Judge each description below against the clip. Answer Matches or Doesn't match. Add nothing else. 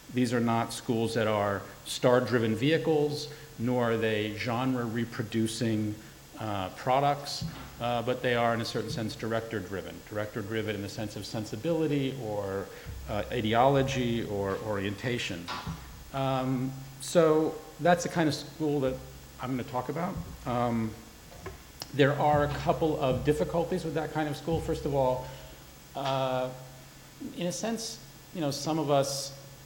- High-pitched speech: Doesn't match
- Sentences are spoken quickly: Doesn't match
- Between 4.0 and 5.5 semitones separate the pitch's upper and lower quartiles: Matches